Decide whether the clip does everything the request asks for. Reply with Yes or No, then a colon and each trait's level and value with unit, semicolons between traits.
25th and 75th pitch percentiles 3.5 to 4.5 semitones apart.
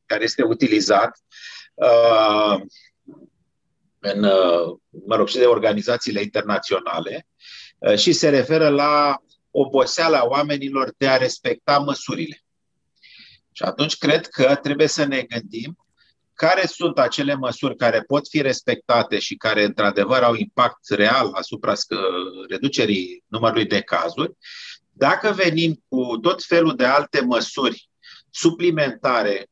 No: wide, 5.6 semitones